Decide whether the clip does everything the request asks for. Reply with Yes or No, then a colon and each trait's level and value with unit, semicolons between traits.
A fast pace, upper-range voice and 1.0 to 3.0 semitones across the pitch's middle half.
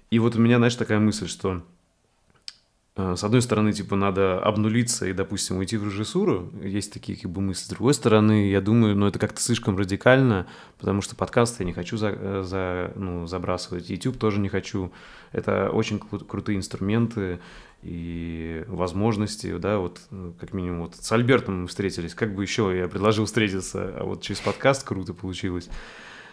No: fast, 180 wpm; low, 100 Hz; average, 2.7 semitones